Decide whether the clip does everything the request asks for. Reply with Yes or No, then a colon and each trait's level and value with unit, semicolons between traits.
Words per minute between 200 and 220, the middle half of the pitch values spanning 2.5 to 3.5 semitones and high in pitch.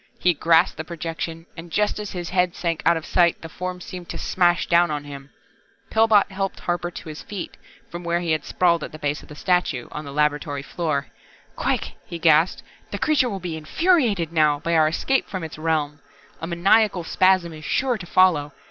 No: fast, 205 wpm; average, 2.8 semitones; medium, 170 Hz